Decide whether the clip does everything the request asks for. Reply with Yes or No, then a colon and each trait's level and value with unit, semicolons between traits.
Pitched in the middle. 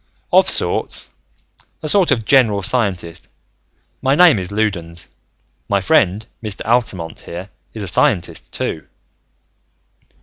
No: low, 100 Hz